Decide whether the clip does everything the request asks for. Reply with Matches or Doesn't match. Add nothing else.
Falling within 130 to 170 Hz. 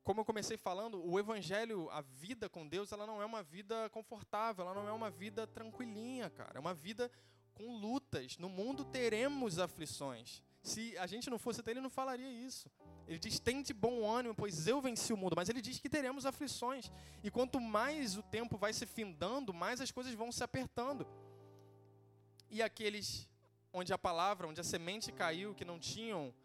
Doesn't match